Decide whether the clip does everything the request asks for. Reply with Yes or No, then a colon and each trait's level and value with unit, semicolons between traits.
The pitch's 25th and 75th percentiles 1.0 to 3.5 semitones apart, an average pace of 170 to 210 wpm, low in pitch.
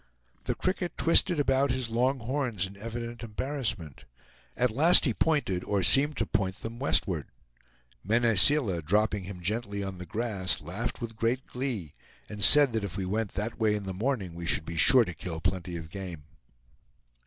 No: average, 5.1 semitones; average, 180 wpm; low, 110 Hz